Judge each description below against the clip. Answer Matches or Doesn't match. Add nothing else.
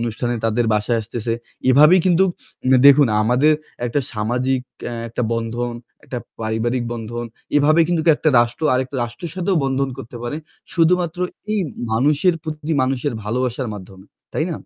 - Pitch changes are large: Doesn't match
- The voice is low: Matches